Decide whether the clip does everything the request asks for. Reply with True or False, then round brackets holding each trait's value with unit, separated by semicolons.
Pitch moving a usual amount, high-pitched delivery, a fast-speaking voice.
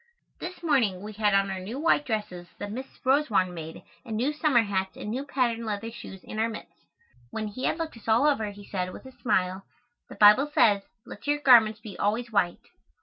True (4.4 semitones; 220 Hz; 210 wpm)